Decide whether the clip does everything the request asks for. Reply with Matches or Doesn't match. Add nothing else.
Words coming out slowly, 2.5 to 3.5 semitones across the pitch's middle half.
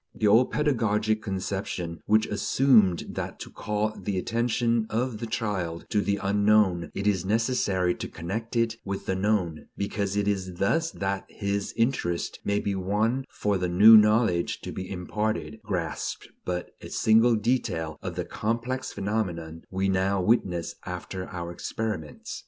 Doesn't match